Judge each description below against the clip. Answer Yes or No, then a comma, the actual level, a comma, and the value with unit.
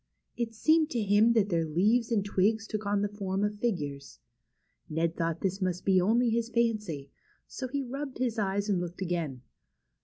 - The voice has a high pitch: Yes, high, 205 Hz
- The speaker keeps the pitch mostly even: No, average, 4.6 semitones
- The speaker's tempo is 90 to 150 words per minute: No, average, 180 wpm